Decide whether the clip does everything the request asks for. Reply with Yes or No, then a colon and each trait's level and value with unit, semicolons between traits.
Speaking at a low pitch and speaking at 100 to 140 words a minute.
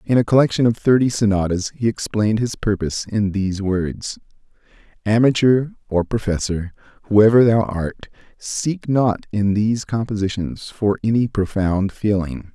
Yes: low, 105 Hz; slow, 135 wpm